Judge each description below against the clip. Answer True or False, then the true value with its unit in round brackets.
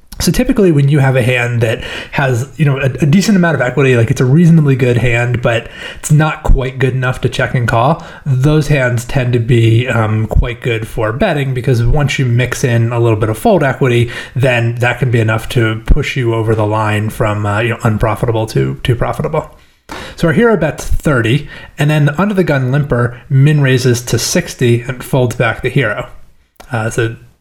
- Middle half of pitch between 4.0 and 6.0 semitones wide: False (3.5 semitones)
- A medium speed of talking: False (210 wpm)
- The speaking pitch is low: True (125 Hz)